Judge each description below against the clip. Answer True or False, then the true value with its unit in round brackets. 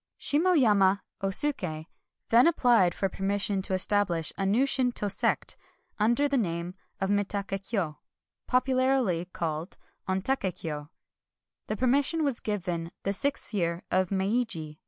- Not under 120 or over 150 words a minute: True (140 wpm)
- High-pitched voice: True (200 Hz)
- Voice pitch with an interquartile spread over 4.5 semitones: True (5.5 semitones)